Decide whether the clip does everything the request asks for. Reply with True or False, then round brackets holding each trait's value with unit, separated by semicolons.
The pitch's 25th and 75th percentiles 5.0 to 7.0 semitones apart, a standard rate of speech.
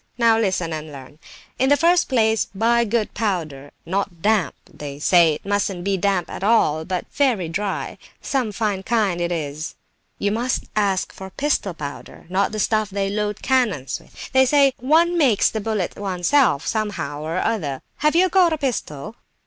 True (5.4 semitones; 175 wpm)